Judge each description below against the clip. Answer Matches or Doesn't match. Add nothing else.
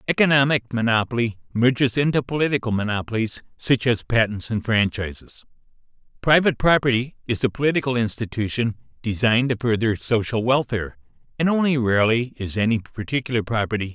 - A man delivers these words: Matches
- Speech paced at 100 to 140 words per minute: Matches